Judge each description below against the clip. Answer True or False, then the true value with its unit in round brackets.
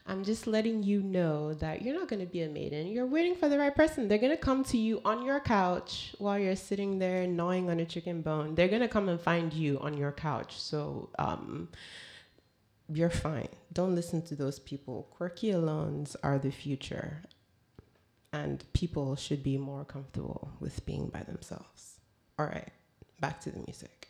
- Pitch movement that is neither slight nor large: False (5.9 semitones)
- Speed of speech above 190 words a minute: False (185 wpm)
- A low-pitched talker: False (175 Hz)